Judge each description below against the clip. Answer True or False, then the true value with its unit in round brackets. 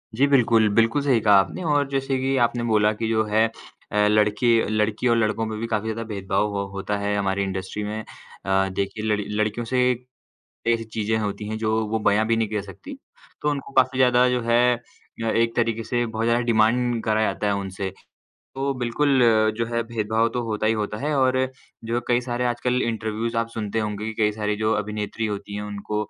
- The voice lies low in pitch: True (110 Hz)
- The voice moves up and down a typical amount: False (2.3 semitones)